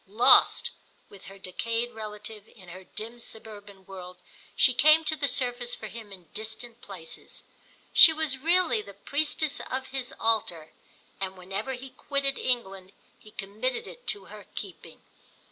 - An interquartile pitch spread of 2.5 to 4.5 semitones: No, average, 5.1 semitones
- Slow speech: No, average, 150 wpm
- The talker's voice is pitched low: No, high, 225 Hz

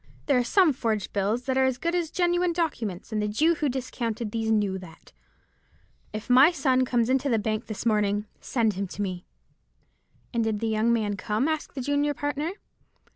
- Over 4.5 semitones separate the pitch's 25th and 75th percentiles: Yes, average, 5.2 semitones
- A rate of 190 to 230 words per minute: Yes, average, 195 wpm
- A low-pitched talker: No, high, 235 Hz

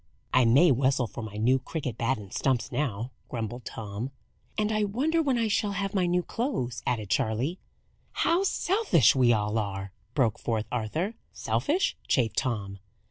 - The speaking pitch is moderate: No, low, 130 Hz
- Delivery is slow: No, average, 165 wpm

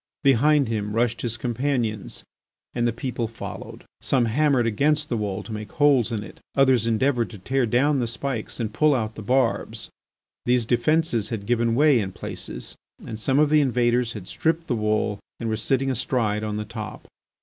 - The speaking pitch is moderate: No, low, 120 Hz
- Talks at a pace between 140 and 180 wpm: No, average, 190 wpm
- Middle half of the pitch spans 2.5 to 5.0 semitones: Yes, average, 3.6 semitones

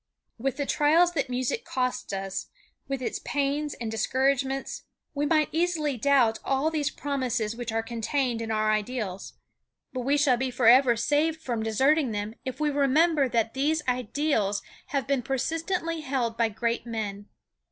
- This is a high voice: Yes, very high, 265 Hz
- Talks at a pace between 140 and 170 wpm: Yes, average, 165 wpm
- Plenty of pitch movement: No, average, 4.2 semitones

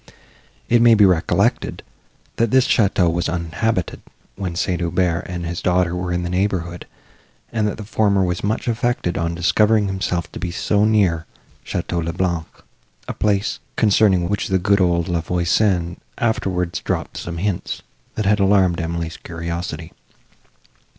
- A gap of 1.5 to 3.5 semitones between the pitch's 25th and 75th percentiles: Yes, average, 3.2 semitones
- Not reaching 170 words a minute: Yes, average, 155 wpm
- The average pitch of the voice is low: Yes, very low, 90 Hz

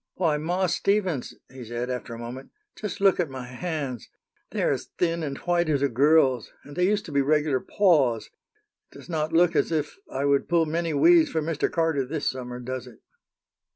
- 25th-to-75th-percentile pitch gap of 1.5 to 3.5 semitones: No, average, 4.8 semitones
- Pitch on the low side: No, medium, 150 Hz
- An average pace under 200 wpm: No, fast, 205 wpm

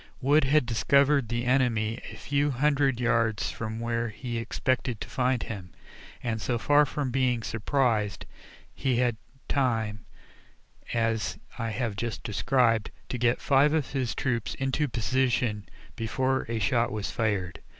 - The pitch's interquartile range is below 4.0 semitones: Yes, average, 2.9 semitones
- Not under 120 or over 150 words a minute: Yes, average, 145 wpm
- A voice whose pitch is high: No, low, 120 Hz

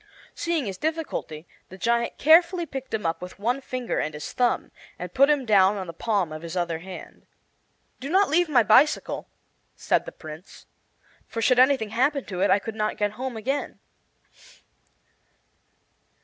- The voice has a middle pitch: No, high, 230 Hz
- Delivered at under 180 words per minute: Yes, average, 170 wpm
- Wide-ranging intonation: Yes, wide, 6.6 semitones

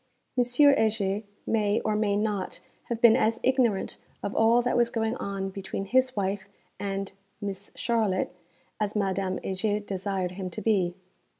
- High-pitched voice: Yes, high, 205 Hz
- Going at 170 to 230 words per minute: No, average, 155 wpm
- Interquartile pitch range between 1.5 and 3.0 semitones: Yes, narrow, 2.6 semitones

